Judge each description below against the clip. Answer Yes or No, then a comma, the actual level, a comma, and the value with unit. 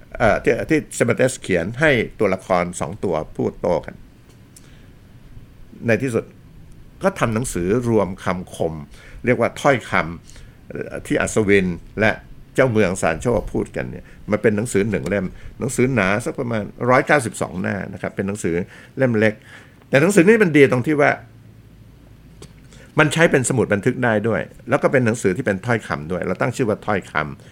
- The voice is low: Yes, low, 115 Hz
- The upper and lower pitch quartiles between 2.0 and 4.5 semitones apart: No, average, 4.9 semitones